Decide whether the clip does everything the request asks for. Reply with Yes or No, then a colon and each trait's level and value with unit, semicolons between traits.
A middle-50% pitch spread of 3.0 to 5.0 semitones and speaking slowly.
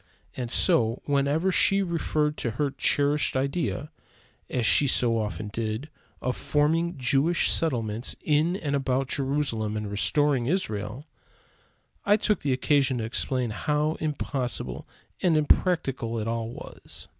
Yes: average, 4.5 semitones; slow, 130 wpm